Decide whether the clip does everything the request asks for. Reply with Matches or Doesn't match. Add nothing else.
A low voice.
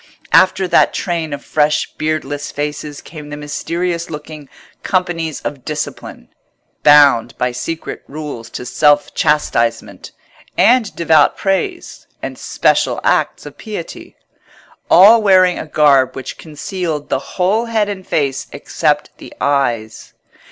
Doesn't match